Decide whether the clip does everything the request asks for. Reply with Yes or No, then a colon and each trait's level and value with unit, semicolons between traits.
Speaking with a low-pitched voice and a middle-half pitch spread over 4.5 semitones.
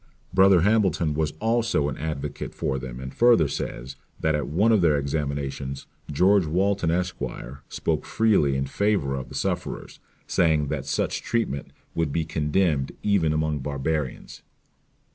Yes: very low, 80 Hz; average, 5.3 semitones